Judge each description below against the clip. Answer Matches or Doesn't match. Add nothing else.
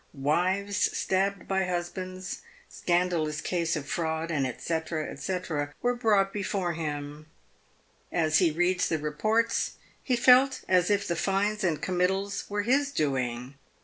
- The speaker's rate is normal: Doesn't match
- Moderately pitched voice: Matches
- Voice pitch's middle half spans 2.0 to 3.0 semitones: Doesn't match